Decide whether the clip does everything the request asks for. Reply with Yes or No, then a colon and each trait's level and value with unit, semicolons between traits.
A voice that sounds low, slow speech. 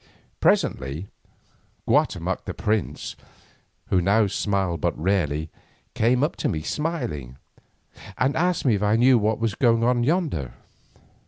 Yes: low, 105 Hz; slow, 130 wpm